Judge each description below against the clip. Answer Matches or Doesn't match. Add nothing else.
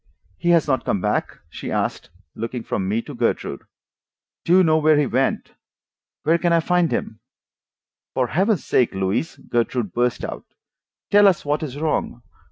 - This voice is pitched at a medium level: Matches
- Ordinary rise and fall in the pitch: Doesn't match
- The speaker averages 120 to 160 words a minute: Doesn't match